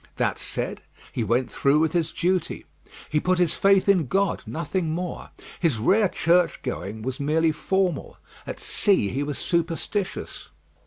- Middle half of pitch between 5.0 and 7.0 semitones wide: No, average, 4.4 semitones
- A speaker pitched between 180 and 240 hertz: No, medium, 165 Hz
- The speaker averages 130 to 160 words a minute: Yes, average, 150 wpm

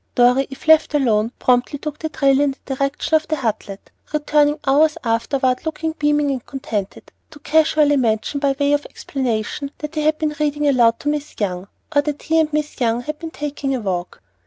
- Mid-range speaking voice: No, very high, 285 Hz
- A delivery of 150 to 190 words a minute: No, average, 200 wpm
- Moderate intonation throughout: Yes, average, 3.4 semitones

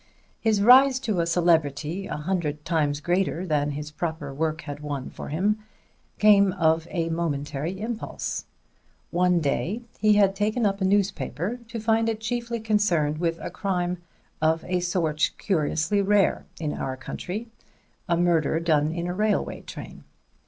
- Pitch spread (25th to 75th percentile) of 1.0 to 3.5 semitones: No, average, 4.9 semitones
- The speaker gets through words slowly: No, average, 155 wpm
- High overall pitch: No, medium, 175 Hz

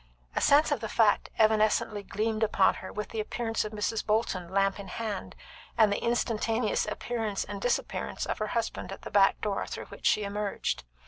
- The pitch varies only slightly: Yes, narrow, 1.9 semitones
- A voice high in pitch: Yes, high, 215 Hz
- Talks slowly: No, average, 190 wpm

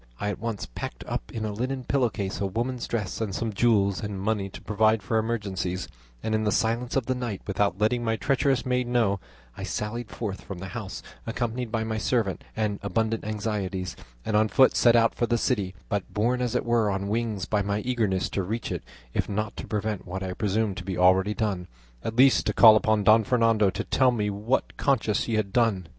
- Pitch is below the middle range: Yes, low, 110 Hz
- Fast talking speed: Yes, fast, 225 wpm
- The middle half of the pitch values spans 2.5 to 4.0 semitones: Yes, average, 2.8 semitones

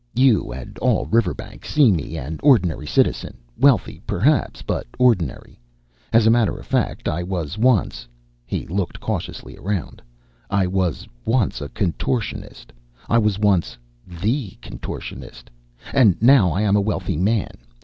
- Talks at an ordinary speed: Yes, average, 145 wpm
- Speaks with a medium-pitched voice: No, low, 100 Hz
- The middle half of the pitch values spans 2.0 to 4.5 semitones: No, average, 5.0 semitones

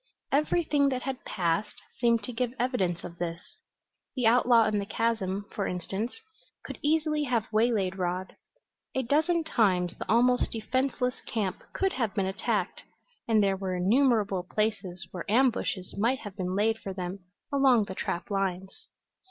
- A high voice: Yes, high, 215 Hz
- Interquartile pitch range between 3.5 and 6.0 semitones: Yes, average, 4.8 semitones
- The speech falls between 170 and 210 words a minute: No, average, 155 wpm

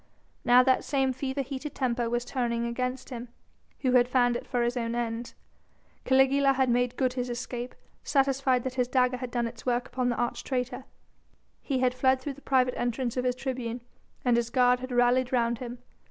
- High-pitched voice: Yes, very high, 250 Hz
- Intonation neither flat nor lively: No, narrow, 1.3 semitones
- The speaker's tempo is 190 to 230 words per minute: Yes, average, 200 wpm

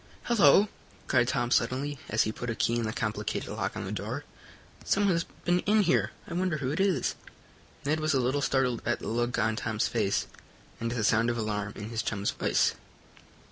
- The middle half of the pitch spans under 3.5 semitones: No, wide, 5.5 semitones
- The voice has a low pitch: Yes, low, 120 Hz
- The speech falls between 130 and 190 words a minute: No, fast, 205 wpm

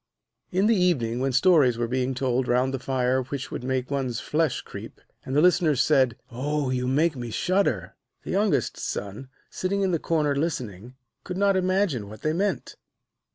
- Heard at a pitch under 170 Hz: Yes, low, 135 Hz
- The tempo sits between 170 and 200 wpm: Yes, average, 175 wpm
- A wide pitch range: Yes, wide, 5.8 semitones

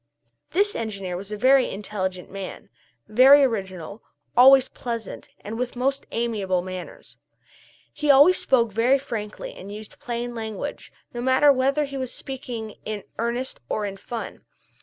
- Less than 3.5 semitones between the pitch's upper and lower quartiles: No, average, 4.2 semitones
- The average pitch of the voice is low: No, high, 235 Hz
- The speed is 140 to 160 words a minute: Yes, average, 150 wpm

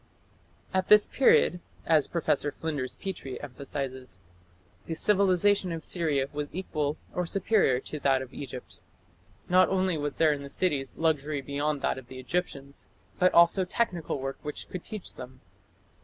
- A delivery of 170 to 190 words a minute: No, average, 155 wpm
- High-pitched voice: No, medium, 150 Hz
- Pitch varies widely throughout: No, average, 4.8 semitones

